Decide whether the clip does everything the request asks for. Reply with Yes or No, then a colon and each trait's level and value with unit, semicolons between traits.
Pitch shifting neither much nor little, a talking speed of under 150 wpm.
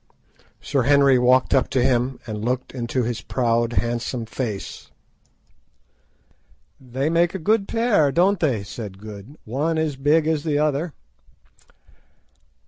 Yes: average, 4.6 semitones; slow, 135 wpm